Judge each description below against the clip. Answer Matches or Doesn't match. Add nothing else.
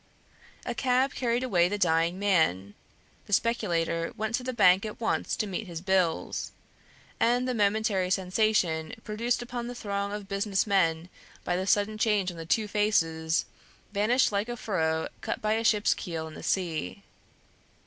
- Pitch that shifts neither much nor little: Matches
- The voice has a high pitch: Matches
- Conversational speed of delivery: Matches